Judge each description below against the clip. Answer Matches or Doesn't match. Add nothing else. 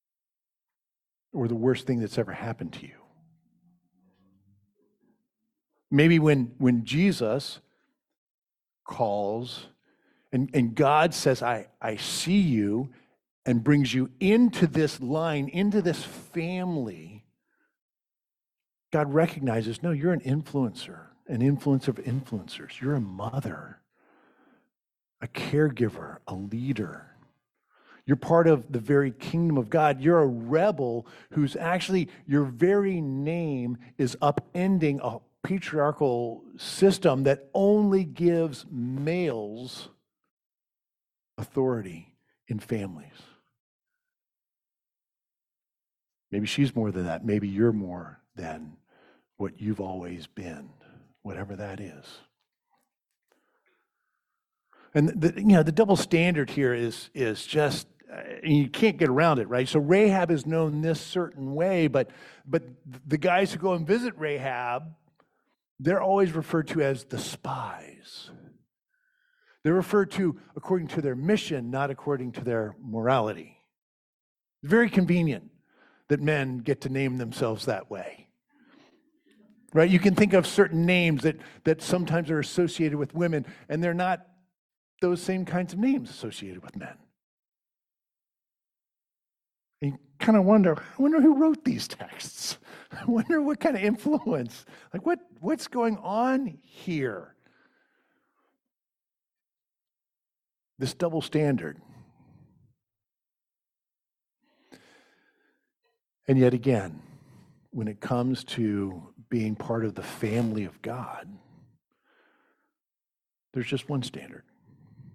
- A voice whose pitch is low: Doesn't match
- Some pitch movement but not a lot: Doesn't match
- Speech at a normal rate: Doesn't match